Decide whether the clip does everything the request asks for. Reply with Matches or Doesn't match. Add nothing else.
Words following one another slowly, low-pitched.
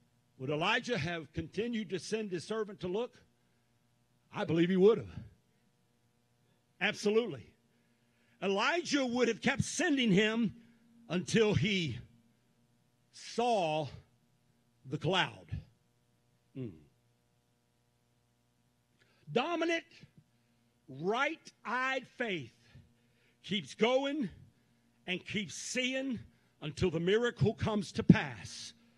Doesn't match